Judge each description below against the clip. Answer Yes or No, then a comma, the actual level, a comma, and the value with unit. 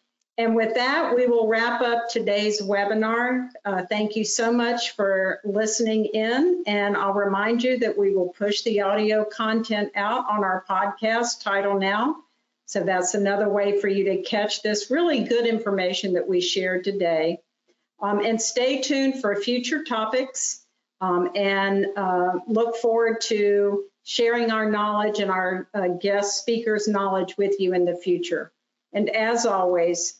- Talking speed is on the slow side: No, average, 160 wpm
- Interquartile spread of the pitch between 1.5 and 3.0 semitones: Yes, average, 2.7 semitones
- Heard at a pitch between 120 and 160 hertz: No, high, 210 Hz